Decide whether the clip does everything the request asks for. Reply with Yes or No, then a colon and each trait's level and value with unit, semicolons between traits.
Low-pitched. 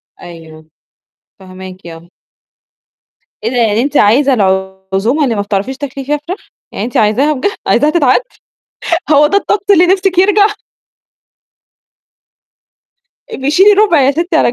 No: very high, 265 Hz